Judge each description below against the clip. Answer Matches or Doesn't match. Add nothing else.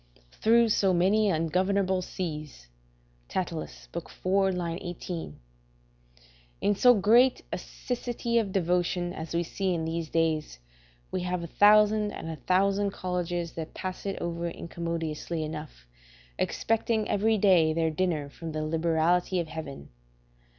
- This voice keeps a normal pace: Doesn't match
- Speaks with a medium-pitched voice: Matches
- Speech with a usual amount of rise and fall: Matches